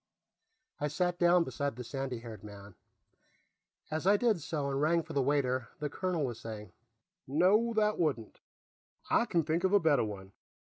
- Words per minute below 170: No, average, 175 wpm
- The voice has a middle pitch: Yes, medium, 150 Hz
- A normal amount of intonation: No, wide, 5.9 semitones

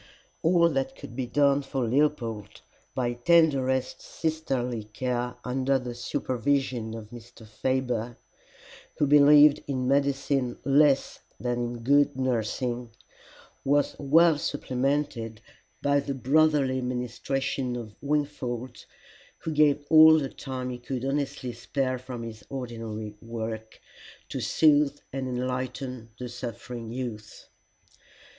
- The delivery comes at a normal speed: No, slow, 115 wpm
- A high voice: No, low, 130 Hz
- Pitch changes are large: No, average, 2.8 semitones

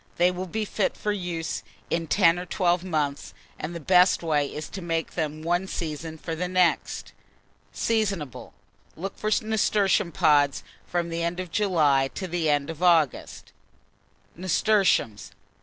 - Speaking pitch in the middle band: Yes, medium, 175 Hz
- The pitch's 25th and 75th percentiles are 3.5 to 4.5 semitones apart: No, average, 2.9 semitones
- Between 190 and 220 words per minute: No, average, 155 wpm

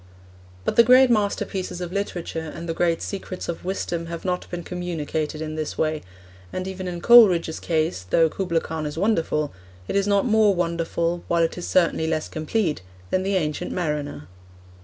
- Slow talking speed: No, average, 180 wpm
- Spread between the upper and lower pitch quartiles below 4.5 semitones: Yes, average, 2.9 semitones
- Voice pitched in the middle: Yes, medium, 170 Hz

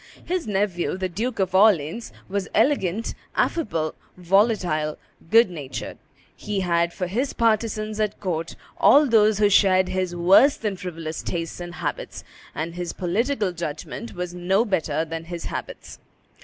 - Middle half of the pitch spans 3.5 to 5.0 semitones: Yes, average, 3.9 semitones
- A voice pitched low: No, medium, 185 Hz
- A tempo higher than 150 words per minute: No, average, 145 wpm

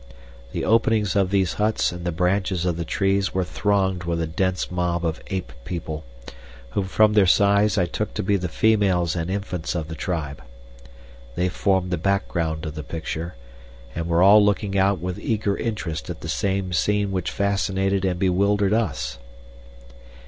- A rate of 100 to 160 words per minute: No, average, 175 wpm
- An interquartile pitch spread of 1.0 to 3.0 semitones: Yes, average, 2.7 semitones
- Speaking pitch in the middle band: No, very low, 95 Hz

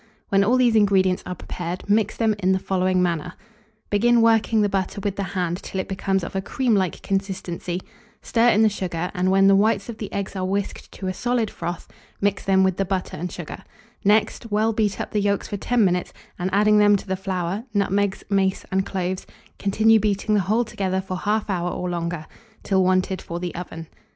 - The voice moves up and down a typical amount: No, narrow, 2.2 semitones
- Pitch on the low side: No, high, 195 Hz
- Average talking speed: No, fast, 210 wpm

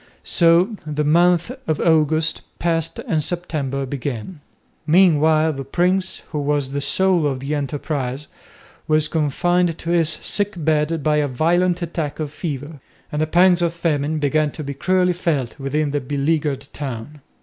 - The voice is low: No, medium, 155 Hz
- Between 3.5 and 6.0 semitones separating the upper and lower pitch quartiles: No, average, 3.0 semitones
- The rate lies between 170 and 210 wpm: No, average, 155 wpm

